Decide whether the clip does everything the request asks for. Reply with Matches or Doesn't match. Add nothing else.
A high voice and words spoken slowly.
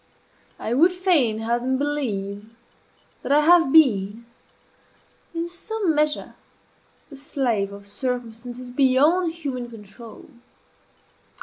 Matches